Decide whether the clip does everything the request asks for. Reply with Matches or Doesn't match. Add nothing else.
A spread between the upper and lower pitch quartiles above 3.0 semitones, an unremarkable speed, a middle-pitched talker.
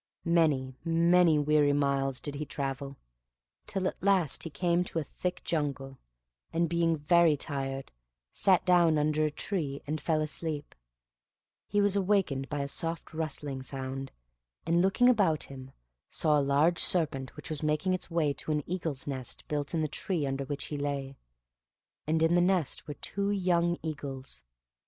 Matches